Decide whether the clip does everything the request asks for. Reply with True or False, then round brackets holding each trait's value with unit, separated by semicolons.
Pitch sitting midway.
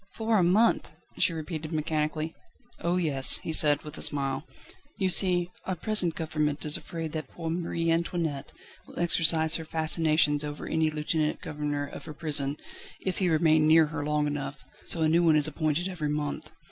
True (155 Hz)